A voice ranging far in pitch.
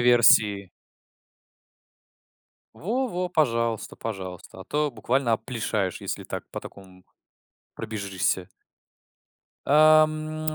Yes: wide, 7.7 semitones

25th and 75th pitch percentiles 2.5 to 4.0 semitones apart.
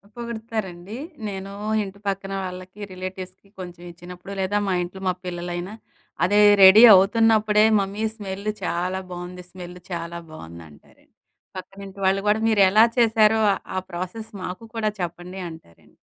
Yes: average, 2.8 semitones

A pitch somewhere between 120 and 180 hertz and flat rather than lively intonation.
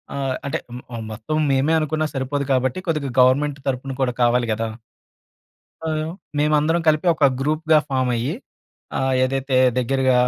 No: low, 135 Hz; average, 3.0 semitones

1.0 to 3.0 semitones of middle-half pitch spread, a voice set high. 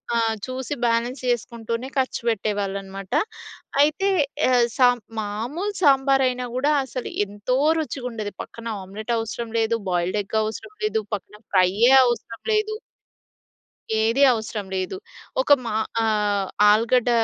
No: average, 3.5 semitones; high, 230 Hz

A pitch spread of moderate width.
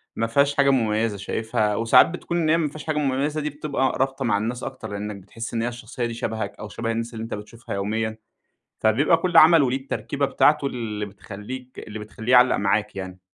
Yes: average, 4.4 semitones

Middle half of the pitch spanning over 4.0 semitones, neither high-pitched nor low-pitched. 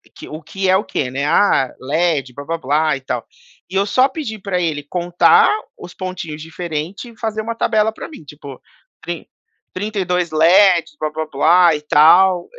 Yes: average, 4.4 semitones; medium, 175 Hz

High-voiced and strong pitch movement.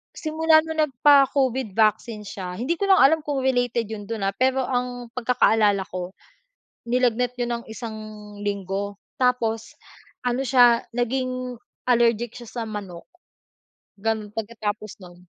No: high, 240 Hz; average, 3.3 semitones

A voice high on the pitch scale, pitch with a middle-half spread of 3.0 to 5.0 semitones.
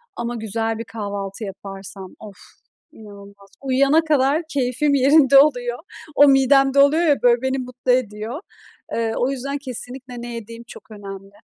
Yes: high, 245 Hz; average, 4.2 semitones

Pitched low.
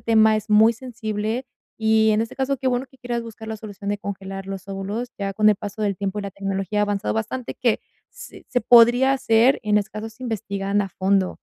No: high, 215 Hz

